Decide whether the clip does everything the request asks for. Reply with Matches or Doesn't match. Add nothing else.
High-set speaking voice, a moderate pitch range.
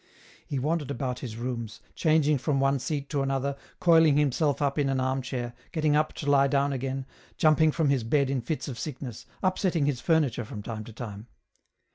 Doesn't match